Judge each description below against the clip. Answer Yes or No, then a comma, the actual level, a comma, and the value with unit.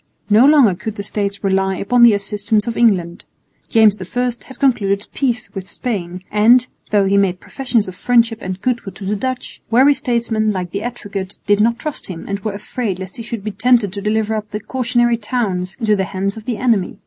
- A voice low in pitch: No, high, 210 Hz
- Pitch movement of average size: Yes, average, 3.3 semitones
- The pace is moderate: No, fast, 210 wpm